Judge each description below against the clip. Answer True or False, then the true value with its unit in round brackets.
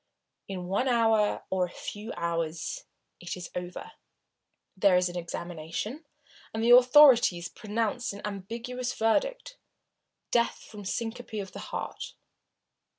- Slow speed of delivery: True (130 wpm)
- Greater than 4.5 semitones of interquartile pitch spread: True (5.0 semitones)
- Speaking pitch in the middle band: False (210 Hz)